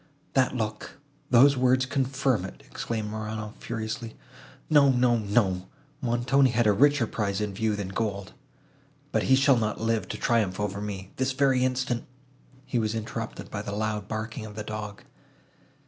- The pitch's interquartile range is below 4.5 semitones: Yes, average, 3.3 semitones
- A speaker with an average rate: Yes, average, 160 wpm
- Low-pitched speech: Yes, low, 110 Hz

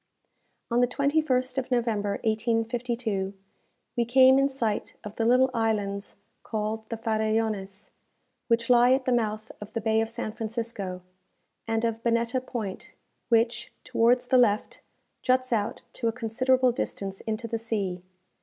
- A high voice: Yes, high, 230 Hz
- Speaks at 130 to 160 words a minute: Yes, average, 145 wpm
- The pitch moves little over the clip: Yes, narrow, 2.3 semitones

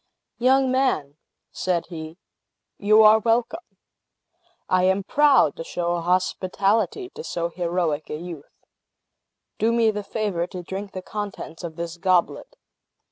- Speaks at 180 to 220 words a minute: No, slow, 135 wpm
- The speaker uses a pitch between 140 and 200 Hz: Yes, medium, 185 Hz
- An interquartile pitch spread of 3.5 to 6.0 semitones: Yes, average, 4.4 semitones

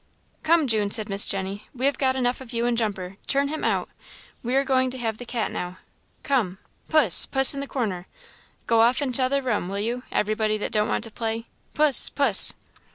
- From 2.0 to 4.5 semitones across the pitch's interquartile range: Yes, average, 3.9 semitones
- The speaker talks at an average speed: No, fast, 210 wpm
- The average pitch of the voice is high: Yes, high, 235 Hz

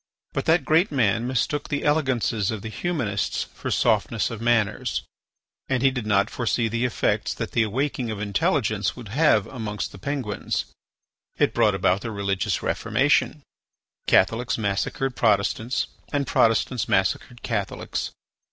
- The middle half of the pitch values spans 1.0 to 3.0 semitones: No, average, 4.2 semitones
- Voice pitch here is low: Yes, low, 115 Hz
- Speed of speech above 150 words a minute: No, average, 145 wpm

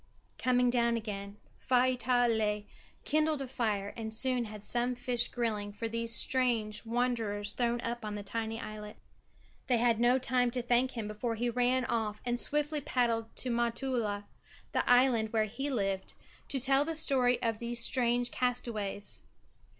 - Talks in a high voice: Yes, high, 235 Hz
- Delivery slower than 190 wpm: Yes, average, 160 wpm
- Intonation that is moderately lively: No, narrow, 2.3 semitones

